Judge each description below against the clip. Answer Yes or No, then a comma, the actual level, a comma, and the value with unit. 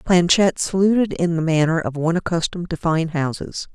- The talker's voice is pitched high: No, medium, 170 Hz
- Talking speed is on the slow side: No, average, 175 wpm